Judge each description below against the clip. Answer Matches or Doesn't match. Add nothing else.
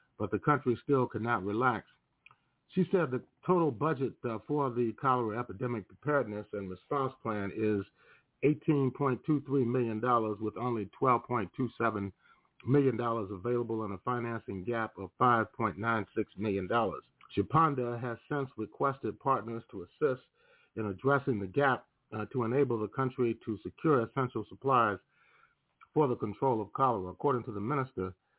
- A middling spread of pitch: Matches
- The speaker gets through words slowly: Matches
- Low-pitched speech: Matches